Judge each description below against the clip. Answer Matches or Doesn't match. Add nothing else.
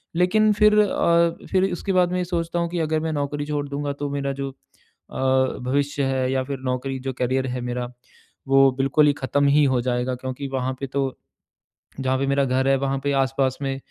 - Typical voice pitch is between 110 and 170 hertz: Matches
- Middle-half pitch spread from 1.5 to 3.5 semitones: Matches